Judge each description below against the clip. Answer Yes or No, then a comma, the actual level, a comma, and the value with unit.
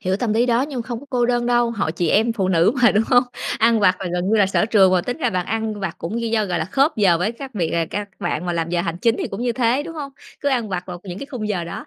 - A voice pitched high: Yes, high, 220 Hz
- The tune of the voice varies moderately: Yes, average, 4.8 semitones